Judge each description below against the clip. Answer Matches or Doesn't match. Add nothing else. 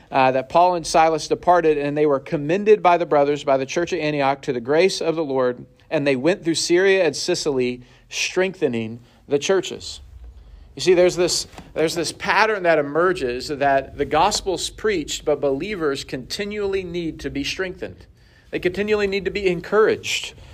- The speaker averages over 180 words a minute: Doesn't match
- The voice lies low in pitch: Doesn't match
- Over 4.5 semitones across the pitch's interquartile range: Matches